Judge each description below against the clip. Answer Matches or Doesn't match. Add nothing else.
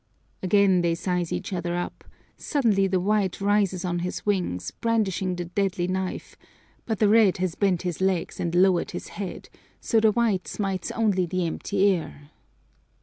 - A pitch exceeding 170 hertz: Matches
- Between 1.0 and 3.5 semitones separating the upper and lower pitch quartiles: Matches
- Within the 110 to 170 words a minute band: Matches